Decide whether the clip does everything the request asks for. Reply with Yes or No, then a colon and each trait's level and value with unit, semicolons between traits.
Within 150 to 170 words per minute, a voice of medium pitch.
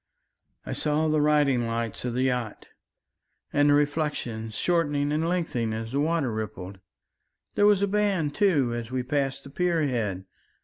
Yes: average, 165 wpm; medium, 145 Hz